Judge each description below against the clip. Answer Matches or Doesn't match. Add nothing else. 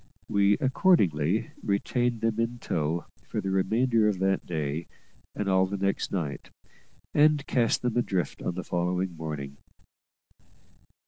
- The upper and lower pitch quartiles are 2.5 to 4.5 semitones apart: Doesn't match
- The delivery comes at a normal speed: Doesn't match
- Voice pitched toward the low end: Matches